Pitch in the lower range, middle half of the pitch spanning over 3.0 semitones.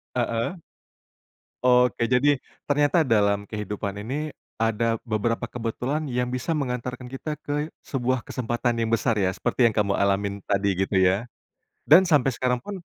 Yes: low, 120 Hz; average, 3.8 semitones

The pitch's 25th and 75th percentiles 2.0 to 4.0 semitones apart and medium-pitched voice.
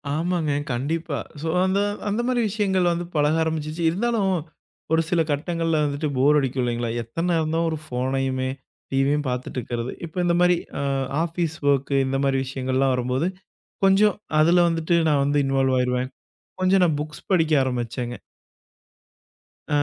No: average, 4.4 semitones; medium, 150 Hz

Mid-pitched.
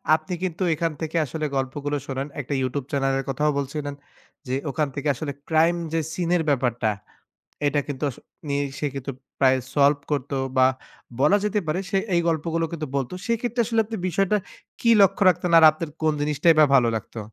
Yes: medium, 150 Hz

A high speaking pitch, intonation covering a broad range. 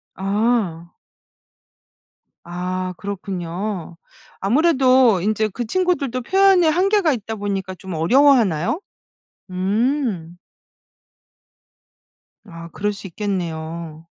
Yes: high, 200 Hz; wide, 6.3 semitones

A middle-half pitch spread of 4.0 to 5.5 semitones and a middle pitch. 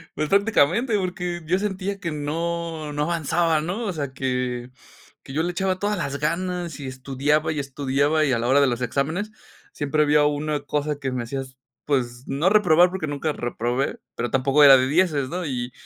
Yes: average, 4.3 semitones; medium, 150 Hz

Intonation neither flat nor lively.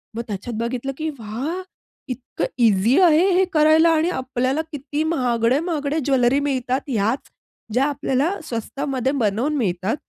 Yes: average, 4.5 semitones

